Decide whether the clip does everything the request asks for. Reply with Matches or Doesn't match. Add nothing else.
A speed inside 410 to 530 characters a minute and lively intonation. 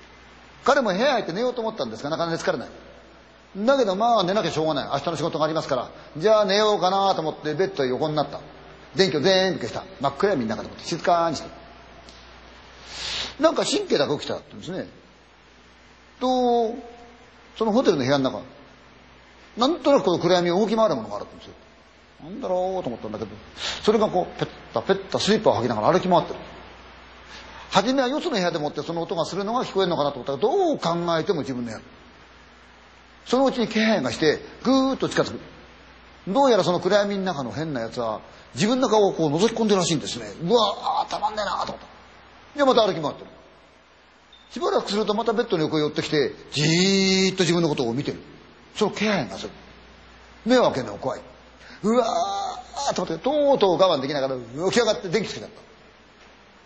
Matches